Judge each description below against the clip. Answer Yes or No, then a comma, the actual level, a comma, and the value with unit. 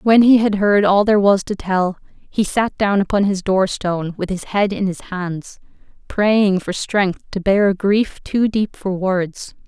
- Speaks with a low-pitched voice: No, high, 195 Hz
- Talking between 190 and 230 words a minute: Yes, fast, 205 wpm